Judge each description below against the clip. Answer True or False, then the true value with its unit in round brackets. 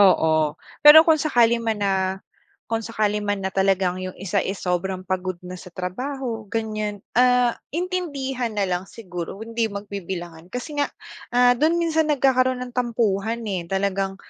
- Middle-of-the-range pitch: False (215 Hz)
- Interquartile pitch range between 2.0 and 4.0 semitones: False (4.7 semitones)